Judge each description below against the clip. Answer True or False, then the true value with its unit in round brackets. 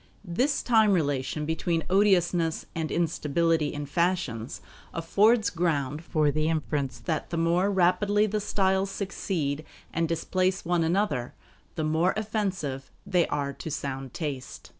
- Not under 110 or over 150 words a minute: True (135 wpm)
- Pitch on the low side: False (165 Hz)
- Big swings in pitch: False (4.3 semitones)